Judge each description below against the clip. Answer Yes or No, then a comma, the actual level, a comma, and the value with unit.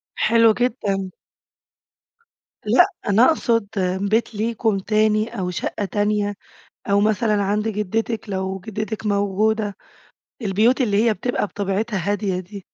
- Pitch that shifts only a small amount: Yes, narrow, 1.9 semitones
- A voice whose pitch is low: No, high, 210 Hz